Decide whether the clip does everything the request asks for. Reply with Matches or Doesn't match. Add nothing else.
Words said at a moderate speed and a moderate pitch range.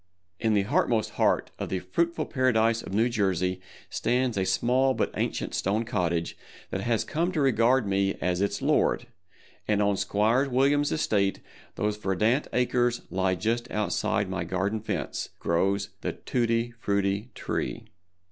Matches